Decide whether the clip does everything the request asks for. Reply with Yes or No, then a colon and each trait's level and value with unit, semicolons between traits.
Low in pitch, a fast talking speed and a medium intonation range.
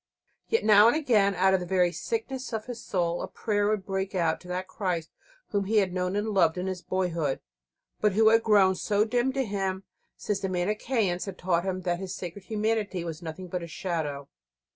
No: high, 190 Hz; fast, 210 wpm; average, 3.0 semitones